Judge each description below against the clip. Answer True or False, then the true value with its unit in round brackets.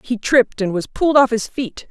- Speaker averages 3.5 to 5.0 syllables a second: False (5.5 syllables/s)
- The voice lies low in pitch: False (240 Hz)